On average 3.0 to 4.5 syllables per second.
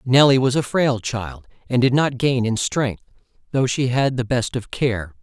Yes: 4.4 syllables/s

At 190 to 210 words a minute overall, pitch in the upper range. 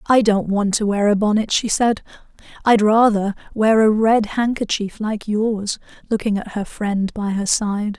No: average, 180 wpm; high, 210 Hz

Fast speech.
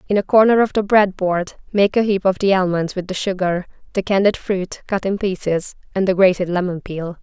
Yes: fast, 225 wpm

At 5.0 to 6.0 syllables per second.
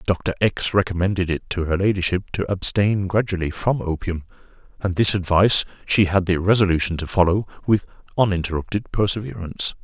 Yes: 5.6 syllables/s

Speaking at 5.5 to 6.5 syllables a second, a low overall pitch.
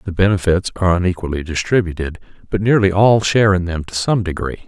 Yes: 6.3 syllables/s; very low, 90 Hz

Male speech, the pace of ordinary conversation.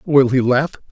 Yes: male; average, 195 wpm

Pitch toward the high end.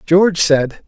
No: medium, 165 Hz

